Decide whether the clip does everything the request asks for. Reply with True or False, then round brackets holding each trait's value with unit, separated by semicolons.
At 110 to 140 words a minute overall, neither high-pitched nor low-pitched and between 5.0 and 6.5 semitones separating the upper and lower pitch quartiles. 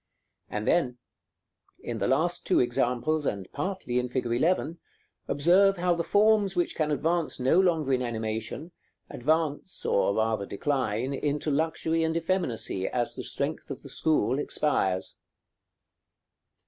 True (135 wpm; 145 Hz; 5.6 semitones)